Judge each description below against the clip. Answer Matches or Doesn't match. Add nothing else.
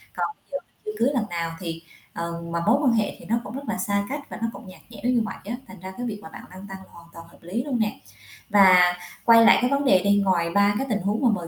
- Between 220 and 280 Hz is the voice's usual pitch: Doesn't match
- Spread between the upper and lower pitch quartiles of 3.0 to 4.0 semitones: Doesn't match